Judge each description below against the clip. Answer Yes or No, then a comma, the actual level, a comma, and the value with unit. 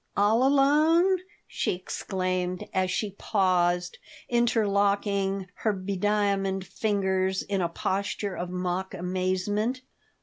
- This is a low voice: No, high, 195 Hz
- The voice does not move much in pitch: Yes, narrow, 2.2 semitones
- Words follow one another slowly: Yes, slow, 100 wpm